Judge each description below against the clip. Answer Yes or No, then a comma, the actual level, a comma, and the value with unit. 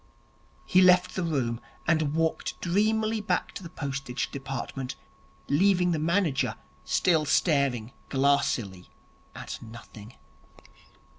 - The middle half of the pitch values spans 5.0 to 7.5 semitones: Yes, average, 5.3 semitones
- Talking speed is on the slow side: Yes, slow, 105 wpm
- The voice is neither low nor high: Yes, medium, 150 Hz